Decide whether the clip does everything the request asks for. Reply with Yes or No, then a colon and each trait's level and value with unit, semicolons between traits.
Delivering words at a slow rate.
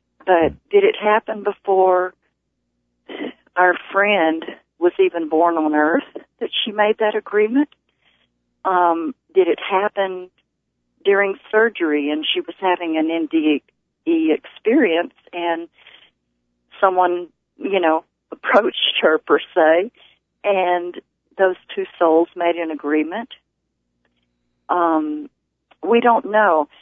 Yes: slow, 110 wpm